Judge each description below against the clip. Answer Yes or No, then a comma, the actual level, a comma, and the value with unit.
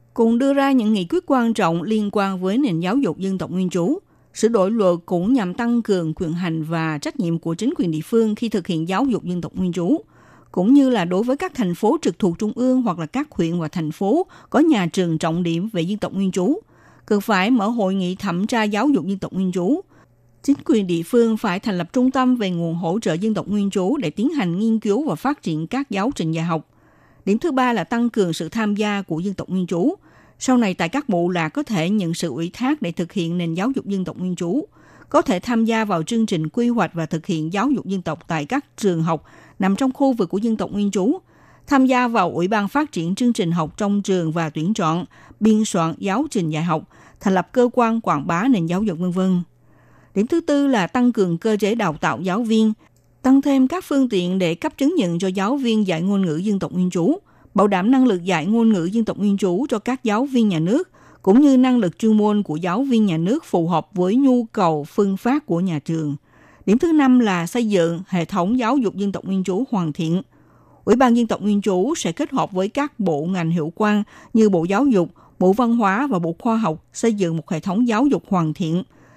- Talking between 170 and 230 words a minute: No, fast, 250 wpm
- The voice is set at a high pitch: Yes, high, 200 Hz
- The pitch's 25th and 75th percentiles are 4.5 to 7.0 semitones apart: Yes, wide, 5.5 semitones